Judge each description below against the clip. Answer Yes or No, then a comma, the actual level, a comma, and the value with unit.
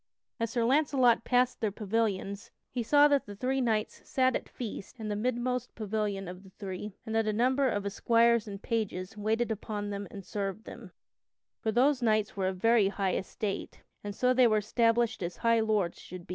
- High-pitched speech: Yes, high, 220 Hz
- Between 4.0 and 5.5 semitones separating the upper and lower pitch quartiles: No, average, 3.0 semitones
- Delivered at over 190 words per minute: Yes, average, 200 wpm